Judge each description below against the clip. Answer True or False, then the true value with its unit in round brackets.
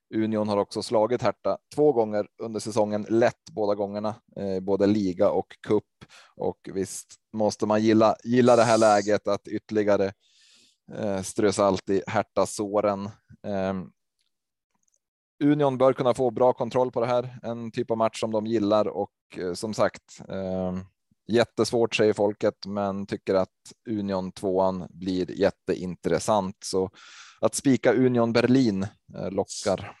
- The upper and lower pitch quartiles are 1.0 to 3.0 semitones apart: True (2.7 semitones)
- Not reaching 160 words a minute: True (130 wpm)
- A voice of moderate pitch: False (105 Hz)